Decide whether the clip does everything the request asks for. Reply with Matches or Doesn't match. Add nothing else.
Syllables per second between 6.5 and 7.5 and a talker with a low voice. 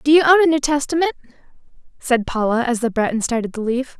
Doesn't match